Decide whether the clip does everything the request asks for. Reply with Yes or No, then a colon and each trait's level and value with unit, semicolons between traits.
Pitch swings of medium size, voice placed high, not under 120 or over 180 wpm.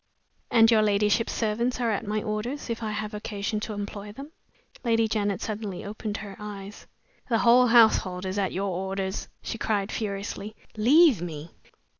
No: narrow, 2.2 semitones; high, 210 Hz; average, 165 wpm